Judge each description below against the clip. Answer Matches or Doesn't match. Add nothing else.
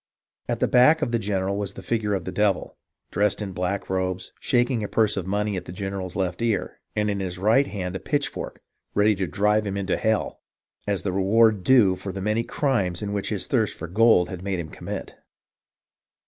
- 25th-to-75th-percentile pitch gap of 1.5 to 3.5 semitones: Matches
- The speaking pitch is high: Doesn't match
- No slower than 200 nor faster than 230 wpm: Matches